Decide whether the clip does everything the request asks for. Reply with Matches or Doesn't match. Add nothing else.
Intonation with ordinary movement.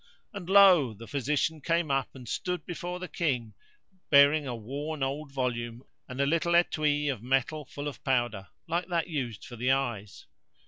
Matches